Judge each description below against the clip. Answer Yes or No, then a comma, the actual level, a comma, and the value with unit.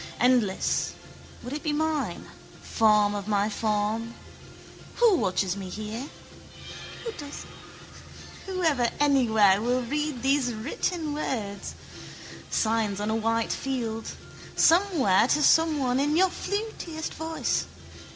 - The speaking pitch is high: Yes, high, 245 Hz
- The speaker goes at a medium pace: No, slow, 110 wpm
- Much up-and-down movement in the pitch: Yes, wide, 5.9 semitones